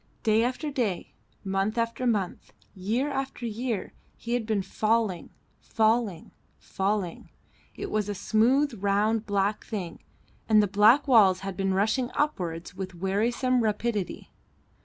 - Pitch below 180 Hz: No, high, 215 Hz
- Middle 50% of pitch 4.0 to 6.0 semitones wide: No, average, 3.5 semitones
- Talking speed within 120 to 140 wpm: Yes, slow, 135 wpm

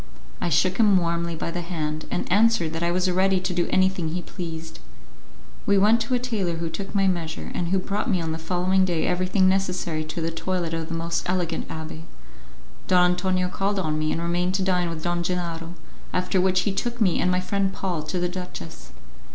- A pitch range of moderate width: No, narrow, 2.1 semitones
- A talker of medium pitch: Yes, medium, 180 Hz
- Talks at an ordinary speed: No, fast, 215 wpm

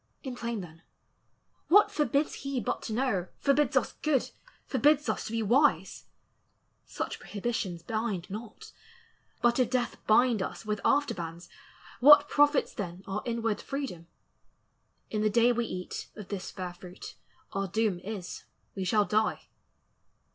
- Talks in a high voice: Yes, high, 225 Hz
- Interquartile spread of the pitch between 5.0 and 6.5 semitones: Yes, wide, 5.4 semitones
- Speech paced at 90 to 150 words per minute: Yes, average, 145 wpm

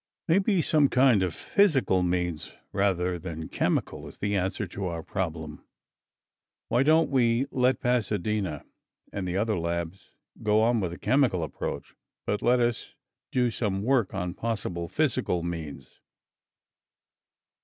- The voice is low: Yes, low, 100 Hz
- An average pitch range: No, wide, 5.8 semitones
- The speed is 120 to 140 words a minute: Yes, slow, 135 wpm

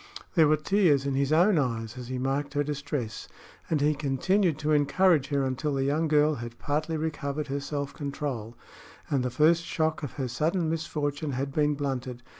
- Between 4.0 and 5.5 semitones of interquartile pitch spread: No, narrow, 2.4 semitones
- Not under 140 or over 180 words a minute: No, average, 190 wpm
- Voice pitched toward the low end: No, medium, 145 Hz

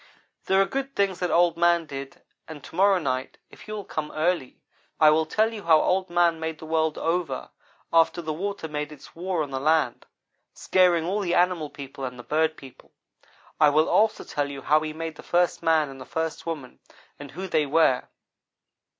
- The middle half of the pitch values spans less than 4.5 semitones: Yes, average, 3.0 semitones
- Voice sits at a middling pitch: Yes, medium, 160 Hz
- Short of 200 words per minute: No, fast, 205 wpm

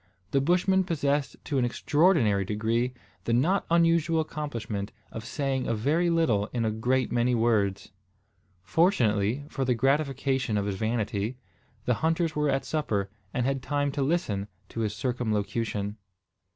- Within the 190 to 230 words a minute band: No, average, 150 wpm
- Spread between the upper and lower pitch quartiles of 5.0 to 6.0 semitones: Yes, wide, 5.4 semitones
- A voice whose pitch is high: No, low, 125 Hz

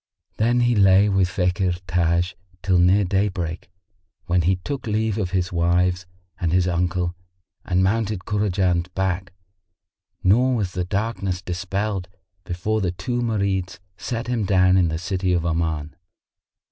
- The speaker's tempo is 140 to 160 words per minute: Yes, average, 145 wpm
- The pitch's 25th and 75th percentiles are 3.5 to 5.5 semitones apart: No, narrow, 2.6 semitones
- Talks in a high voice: No, very low, 95 Hz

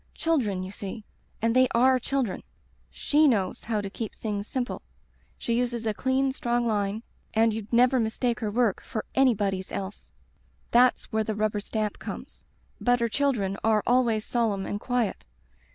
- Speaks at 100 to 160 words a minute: Yes, average, 155 wpm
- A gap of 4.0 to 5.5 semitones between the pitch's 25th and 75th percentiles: No, average, 3.0 semitones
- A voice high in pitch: Yes, high, 225 Hz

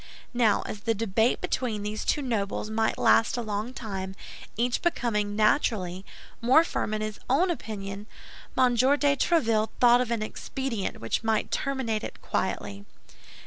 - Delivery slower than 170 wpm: Yes, average, 150 wpm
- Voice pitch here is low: No, high, 225 Hz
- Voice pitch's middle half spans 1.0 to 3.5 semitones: Yes, average, 3.1 semitones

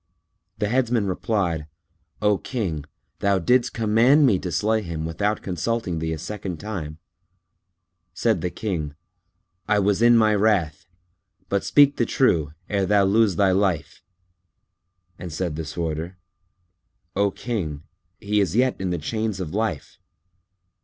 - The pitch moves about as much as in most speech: Yes, average, 4.6 semitones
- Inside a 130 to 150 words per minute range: Yes, average, 140 wpm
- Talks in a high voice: No, low, 100 Hz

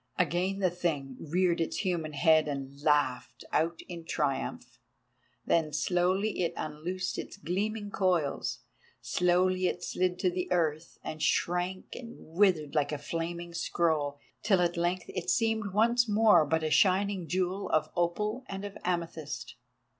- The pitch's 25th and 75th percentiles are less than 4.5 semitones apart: Yes, average, 3.0 semitones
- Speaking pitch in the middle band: Yes, medium, 175 Hz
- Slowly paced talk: No, average, 145 wpm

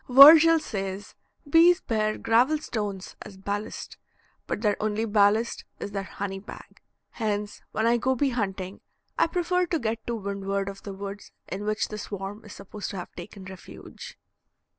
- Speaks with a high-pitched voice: Yes, high, 210 Hz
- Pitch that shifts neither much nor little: Yes, average, 3.3 semitones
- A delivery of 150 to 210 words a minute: Yes, average, 165 wpm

